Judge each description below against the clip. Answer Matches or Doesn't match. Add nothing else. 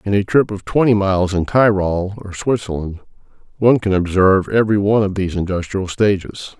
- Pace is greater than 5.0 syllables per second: Matches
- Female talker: Doesn't match